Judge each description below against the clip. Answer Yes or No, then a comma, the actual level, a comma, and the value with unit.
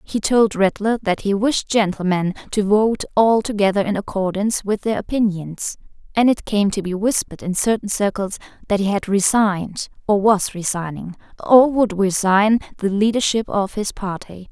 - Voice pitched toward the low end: No, high, 205 Hz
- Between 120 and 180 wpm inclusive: Yes, average, 160 wpm